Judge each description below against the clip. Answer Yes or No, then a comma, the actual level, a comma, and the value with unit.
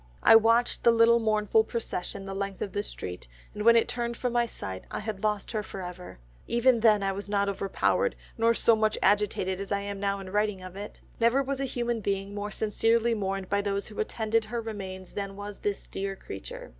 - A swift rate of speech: Yes, fast, 225 wpm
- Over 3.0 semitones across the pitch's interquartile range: No, average, 2.7 semitones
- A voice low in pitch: No, high, 210 Hz